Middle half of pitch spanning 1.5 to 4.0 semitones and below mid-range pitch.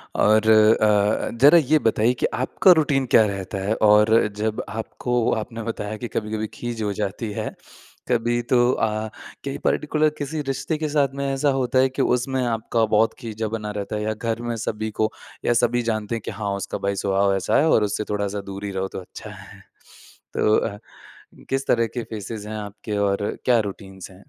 Yes: average, 2.9 semitones; low, 110 Hz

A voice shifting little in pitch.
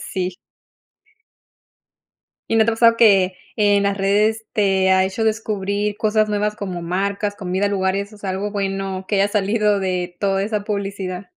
Yes: narrow, 1.7 semitones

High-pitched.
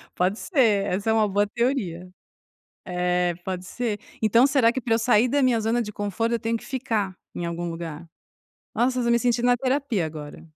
Yes: high, 220 Hz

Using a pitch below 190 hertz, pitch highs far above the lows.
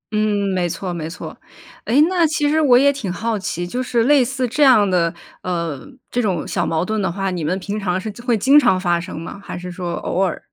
No: high, 200 Hz; wide, 5.7 semitones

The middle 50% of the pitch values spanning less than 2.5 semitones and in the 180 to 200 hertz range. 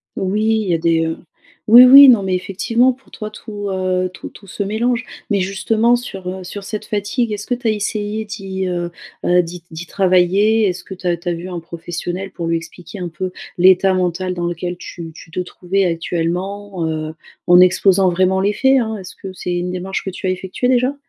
No: average, 2.9 semitones; high, 190 Hz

